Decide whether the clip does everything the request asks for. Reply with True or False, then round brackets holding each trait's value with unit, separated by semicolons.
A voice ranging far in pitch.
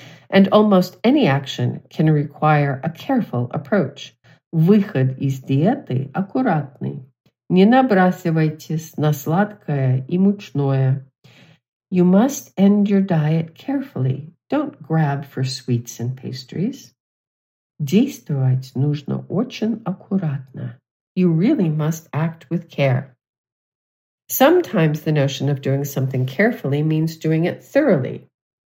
True (5.9 semitones)